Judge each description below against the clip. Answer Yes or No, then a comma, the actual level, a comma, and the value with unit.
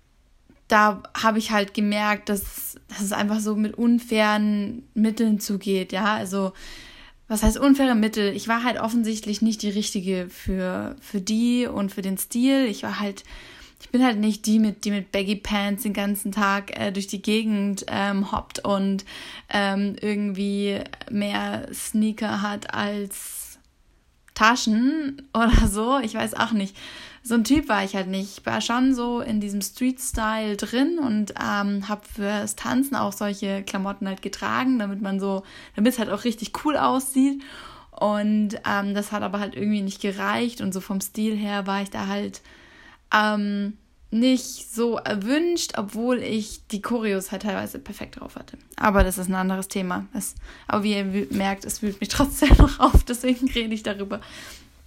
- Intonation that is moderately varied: No, narrow, 2.3 semitones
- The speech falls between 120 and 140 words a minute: No, average, 170 wpm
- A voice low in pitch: No, high, 210 Hz